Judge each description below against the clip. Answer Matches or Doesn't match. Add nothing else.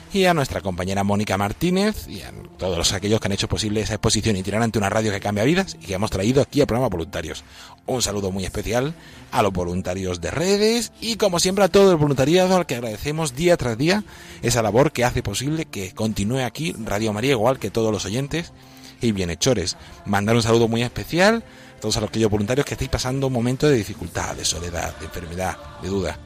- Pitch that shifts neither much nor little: Doesn't match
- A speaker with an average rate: Doesn't match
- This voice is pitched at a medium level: Doesn't match